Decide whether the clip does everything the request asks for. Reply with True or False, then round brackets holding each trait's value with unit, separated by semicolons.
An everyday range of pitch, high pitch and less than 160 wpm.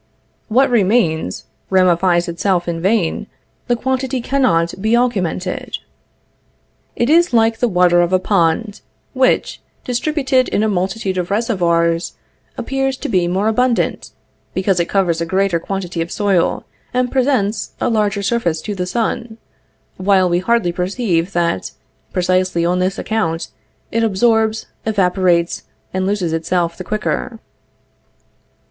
True (4.6 semitones; 195 Hz; 135 wpm)